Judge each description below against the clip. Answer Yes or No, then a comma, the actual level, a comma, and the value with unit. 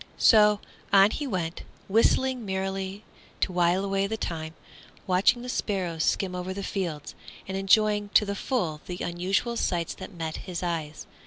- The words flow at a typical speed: Yes, average, 160 wpm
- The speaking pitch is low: No, high, 190 Hz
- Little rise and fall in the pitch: No, average, 3.1 semitones